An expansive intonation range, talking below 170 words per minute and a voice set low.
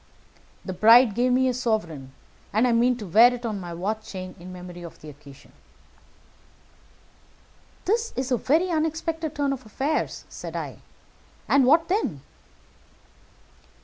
No: wide, 7.0 semitones; average, 145 wpm; high, 240 Hz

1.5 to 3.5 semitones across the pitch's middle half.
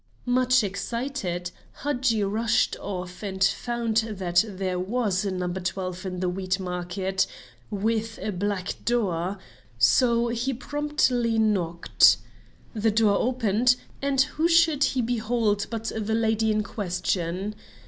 No: average, 4.2 semitones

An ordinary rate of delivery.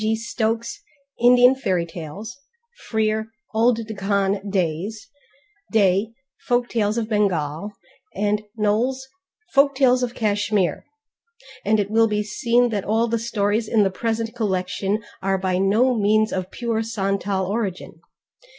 No: slow, 130 wpm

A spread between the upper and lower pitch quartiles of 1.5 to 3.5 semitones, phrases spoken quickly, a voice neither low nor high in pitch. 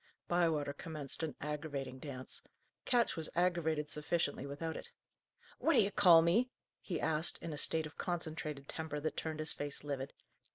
No: narrow, 2.6 semitones; average, 160 wpm; medium, 155 Hz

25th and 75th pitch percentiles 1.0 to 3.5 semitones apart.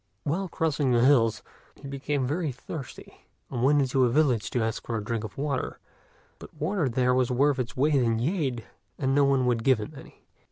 Yes: average, 3.0 semitones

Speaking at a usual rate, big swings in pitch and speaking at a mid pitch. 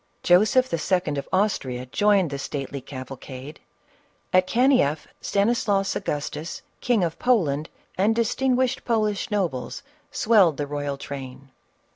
No: slow, 115 wpm; wide, 7.2 semitones; medium, 175 Hz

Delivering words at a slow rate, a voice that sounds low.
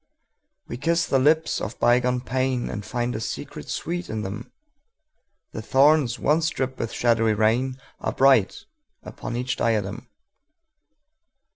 Yes: slow, 120 wpm; low, 125 Hz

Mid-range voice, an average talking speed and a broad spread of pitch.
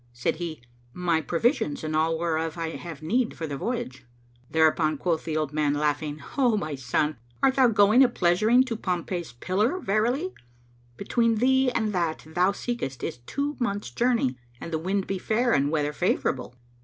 Yes: medium, 175 Hz; average, 180 wpm; wide, 6.9 semitones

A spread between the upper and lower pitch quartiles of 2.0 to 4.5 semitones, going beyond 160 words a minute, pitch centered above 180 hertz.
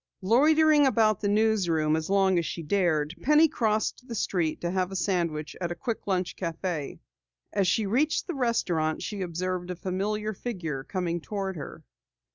Yes: average, 4.2 semitones; average, 170 wpm; high, 190 Hz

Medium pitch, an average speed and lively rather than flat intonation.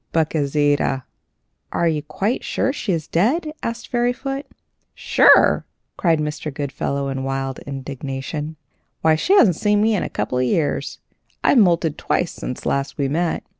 Yes: medium, 155 Hz; average, 160 wpm; wide, 6.8 semitones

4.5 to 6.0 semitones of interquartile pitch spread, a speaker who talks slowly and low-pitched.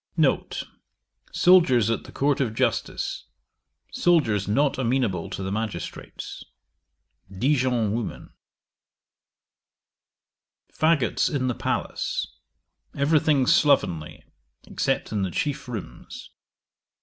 Yes: wide, 5.5 semitones; slow, 95 wpm; low, 125 Hz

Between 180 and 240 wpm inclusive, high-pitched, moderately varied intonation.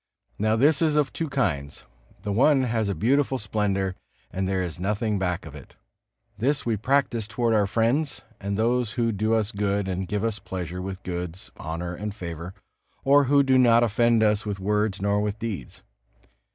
No: average, 185 wpm; low, 105 Hz; average, 3.7 semitones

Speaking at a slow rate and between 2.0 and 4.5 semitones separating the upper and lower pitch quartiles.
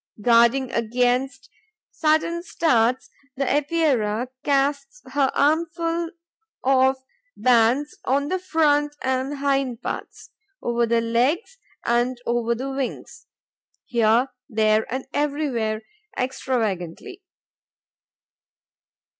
Yes: slow, 90 wpm; average, 3.7 semitones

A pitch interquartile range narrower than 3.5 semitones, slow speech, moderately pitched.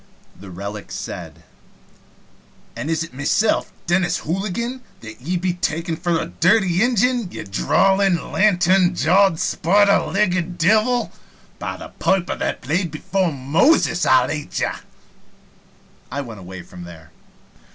No: average, 5.2 semitones; slow, 130 wpm; medium, 175 Hz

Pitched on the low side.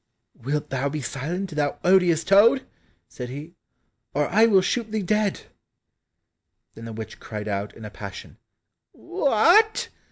No: medium, 165 Hz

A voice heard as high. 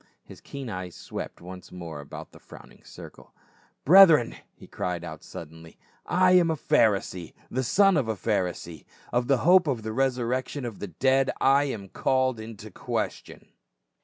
No: low, 120 Hz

